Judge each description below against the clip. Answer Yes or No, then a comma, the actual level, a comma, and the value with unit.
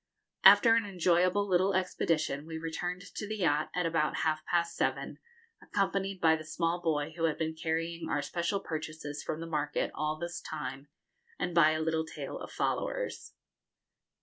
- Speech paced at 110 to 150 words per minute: No, average, 170 wpm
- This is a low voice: No, medium, 165 Hz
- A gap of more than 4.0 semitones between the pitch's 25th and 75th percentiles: No, narrow, 2.4 semitones